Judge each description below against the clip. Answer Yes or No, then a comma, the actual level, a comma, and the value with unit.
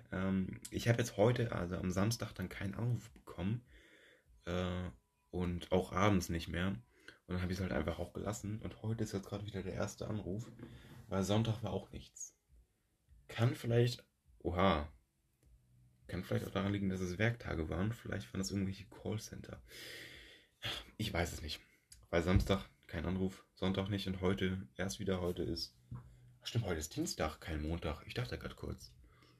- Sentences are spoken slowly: No, average, 170 wpm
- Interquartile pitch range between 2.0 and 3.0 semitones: No, average, 3.5 semitones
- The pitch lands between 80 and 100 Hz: Yes, very low, 95 Hz